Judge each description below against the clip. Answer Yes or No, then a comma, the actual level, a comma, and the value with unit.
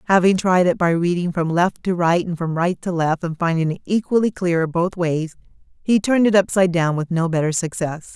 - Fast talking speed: Yes, fast, 220 wpm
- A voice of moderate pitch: Yes, medium, 175 Hz